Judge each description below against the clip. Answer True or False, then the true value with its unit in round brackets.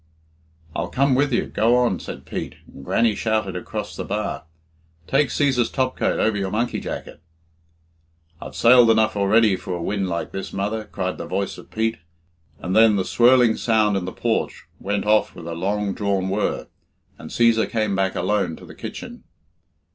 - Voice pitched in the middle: False (105 Hz)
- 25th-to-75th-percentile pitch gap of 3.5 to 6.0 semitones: False (3.1 semitones)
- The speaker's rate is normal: True (180 wpm)